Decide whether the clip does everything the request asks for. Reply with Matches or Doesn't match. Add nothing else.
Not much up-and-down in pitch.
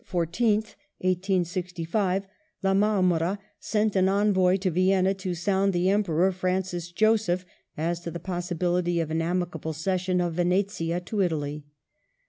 Matches